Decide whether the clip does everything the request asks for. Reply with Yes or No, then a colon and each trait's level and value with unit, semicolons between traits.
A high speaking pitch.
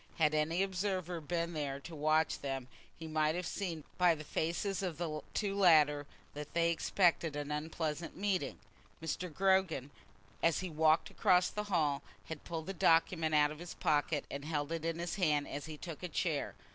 No: medium, 160 Hz